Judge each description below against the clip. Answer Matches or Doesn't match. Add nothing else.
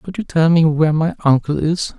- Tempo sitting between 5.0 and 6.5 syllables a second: Matches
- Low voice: Doesn't match